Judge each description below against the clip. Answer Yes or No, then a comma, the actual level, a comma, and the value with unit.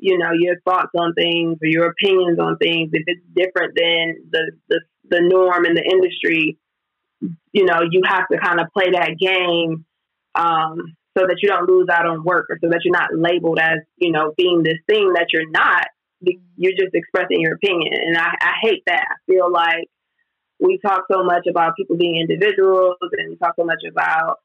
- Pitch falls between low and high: Yes, medium, 175 Hz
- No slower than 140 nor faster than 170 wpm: No, fast, 205 wpm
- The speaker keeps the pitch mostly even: Yes, narrow, 2.0 semitones